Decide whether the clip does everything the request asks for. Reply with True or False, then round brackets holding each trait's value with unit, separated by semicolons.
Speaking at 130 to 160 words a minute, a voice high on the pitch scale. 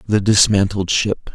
False (135 wpm; 100 Hz)